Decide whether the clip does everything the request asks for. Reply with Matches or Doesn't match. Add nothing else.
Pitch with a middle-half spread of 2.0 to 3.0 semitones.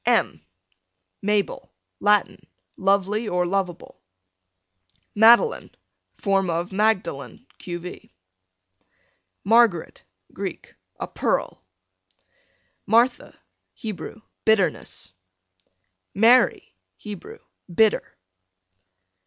Doesn't match